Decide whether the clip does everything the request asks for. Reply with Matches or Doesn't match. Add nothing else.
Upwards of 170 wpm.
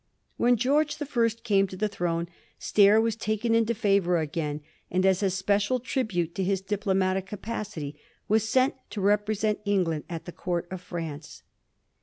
Doesn't match